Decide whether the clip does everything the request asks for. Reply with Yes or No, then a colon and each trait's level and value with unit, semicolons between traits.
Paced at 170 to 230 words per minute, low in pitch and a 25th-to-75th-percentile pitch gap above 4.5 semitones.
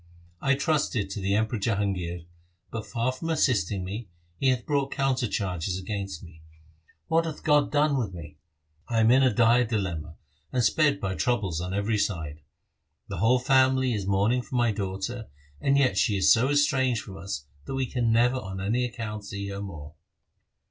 Yes: average, 185 wpm; low, 110 Hz; average, 4.9 semitones